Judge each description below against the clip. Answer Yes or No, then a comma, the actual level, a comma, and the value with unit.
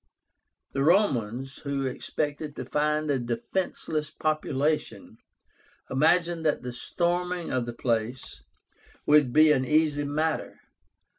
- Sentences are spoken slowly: Yes, slow, 115 wpm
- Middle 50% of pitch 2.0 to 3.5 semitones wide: Yes, average, 3.2 semitones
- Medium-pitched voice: Yes, medium, 150 Hz